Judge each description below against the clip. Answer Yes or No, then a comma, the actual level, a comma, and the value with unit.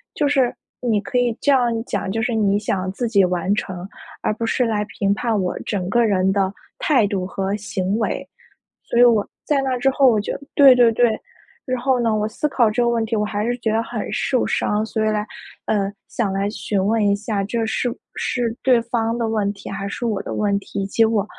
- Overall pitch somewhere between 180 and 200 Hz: No, high, 220 Hz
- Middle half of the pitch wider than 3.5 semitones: No, average, 3.0 semitones